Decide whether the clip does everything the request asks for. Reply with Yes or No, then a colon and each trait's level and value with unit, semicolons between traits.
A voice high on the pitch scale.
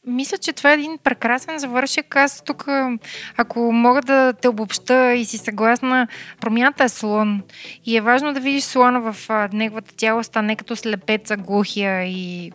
Yes: high, 240 Hz